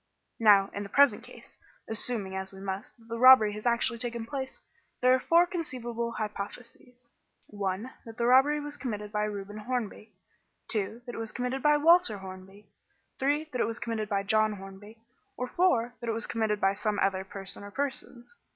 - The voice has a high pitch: Yes, high, 225 Hz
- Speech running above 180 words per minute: Yes, average, 190 wpm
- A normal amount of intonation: Yes, average, 3.5 semitones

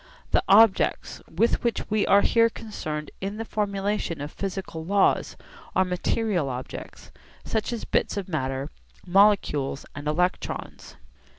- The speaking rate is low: Yes, slow, 130 wpm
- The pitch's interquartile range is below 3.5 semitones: No, average, 5.3 semitones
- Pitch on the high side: Yes, high, 195 Hz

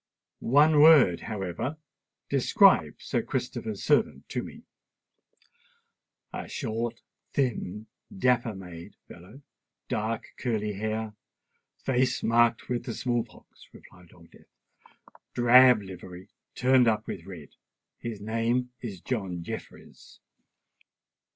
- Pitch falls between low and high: No, low, 110 Hz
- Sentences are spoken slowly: Yes, slow, 95 wpm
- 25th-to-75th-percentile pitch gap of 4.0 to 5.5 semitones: Yes, average, 4.3 semitones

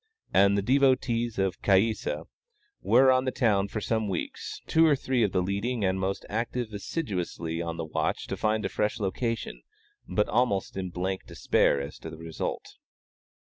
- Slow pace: No, average, 175 wpm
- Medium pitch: No, low, 100 Hz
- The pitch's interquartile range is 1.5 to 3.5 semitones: No, average, 4.1 semitones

